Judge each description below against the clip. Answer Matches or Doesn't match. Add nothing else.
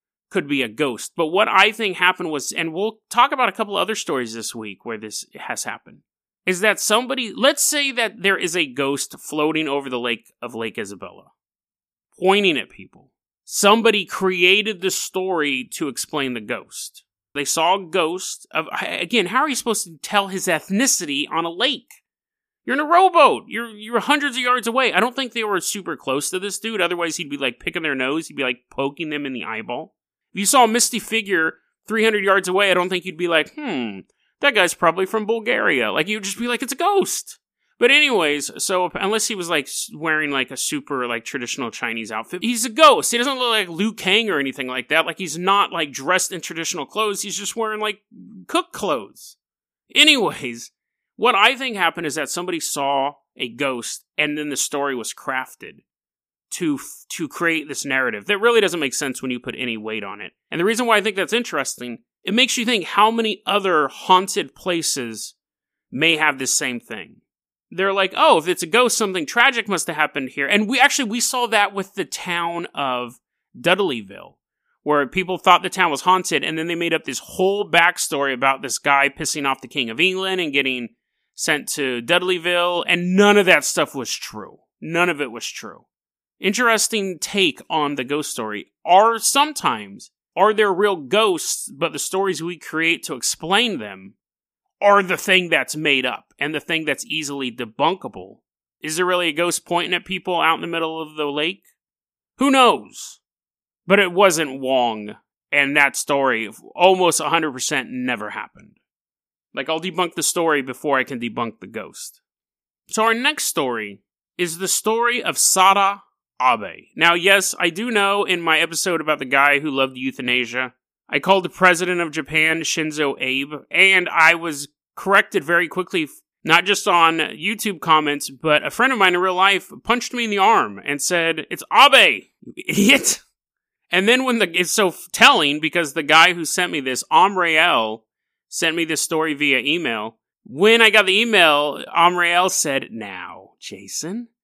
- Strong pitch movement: Matches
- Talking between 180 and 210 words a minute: Matches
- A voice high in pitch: Doesn't match